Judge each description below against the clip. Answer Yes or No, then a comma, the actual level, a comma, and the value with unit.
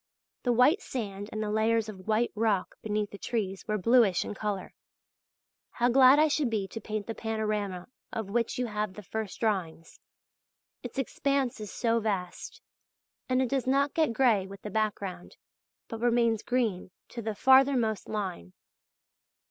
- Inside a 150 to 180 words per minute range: Yes, average, 165 wpm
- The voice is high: Yes, high, 220 Hz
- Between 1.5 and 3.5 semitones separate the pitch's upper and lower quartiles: Yes, average, 3.1 semitones